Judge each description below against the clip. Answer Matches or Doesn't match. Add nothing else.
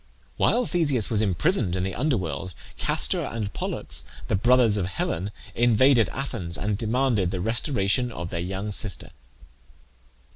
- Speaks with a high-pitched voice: Doesn't match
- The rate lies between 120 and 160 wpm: Matches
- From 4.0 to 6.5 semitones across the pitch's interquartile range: Matches